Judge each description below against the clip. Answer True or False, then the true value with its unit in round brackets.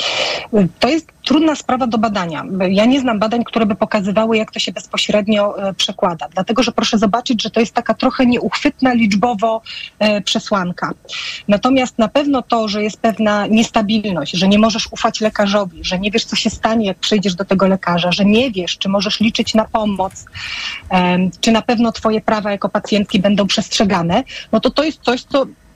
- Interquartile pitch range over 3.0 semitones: False (2.4 semitones)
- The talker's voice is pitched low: False (220 Hz)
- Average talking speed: False (180 wpm)